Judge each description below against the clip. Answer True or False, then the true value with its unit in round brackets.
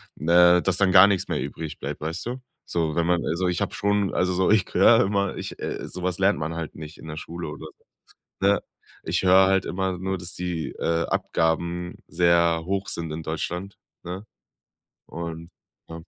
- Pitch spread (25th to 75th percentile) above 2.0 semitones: True (2.5 semitones)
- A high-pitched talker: False (90 Hz)